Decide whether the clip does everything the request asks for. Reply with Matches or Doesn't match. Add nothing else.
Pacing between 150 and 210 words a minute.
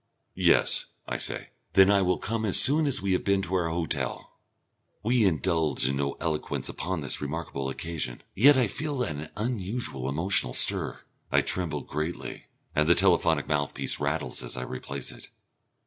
Matches